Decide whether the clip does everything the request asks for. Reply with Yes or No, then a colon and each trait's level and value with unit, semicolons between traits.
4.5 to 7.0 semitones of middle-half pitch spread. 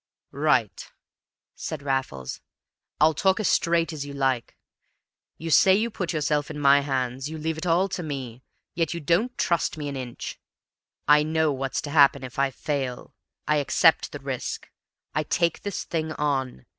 No: average, 3.3 semitones